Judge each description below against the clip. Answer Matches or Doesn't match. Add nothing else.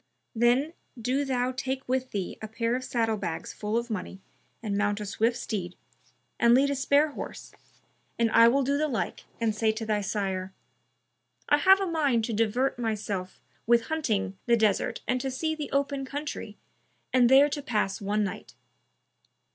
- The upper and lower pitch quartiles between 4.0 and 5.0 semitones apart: Matches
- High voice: Matches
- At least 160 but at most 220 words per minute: Matches